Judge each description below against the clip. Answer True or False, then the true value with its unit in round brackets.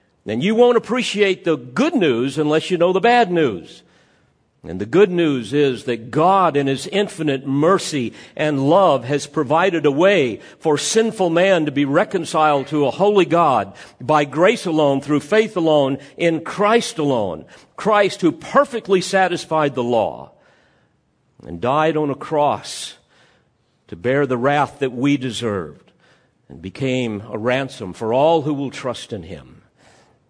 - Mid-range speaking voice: True (155 Hz)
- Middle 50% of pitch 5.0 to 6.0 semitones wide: True (5.3 semitones)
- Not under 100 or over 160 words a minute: True (155 wpm)